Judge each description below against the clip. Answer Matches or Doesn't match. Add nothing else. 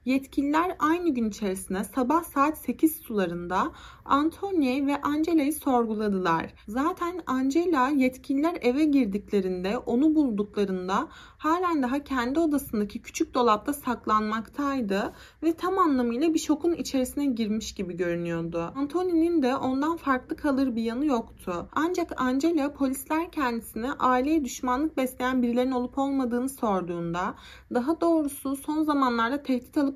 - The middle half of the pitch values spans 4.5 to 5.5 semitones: Matches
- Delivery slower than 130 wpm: Matches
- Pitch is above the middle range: Matches